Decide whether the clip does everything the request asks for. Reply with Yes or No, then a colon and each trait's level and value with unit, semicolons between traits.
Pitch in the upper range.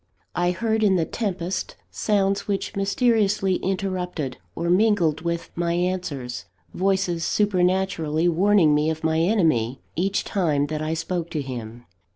No: medium, 175 Hz